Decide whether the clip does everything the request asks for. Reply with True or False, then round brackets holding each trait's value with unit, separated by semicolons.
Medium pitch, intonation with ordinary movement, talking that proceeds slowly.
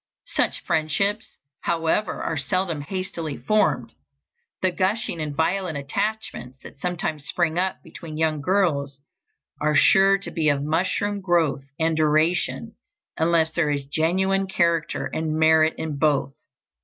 True (160 Hz; 3.5 semitones; 130 wpm)